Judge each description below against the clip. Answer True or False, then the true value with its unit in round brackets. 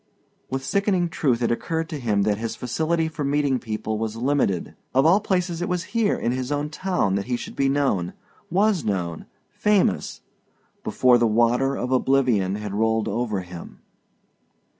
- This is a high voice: False (130 Hz)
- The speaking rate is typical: True (170 wpm)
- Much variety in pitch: True (6.6 semitones)